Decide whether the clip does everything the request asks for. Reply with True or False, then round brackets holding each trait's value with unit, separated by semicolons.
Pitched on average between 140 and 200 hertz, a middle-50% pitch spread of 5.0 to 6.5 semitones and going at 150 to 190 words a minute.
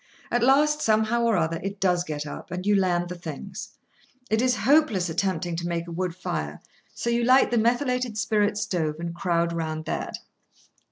True (190 Hz; 5.5 semitones; 185 wpm)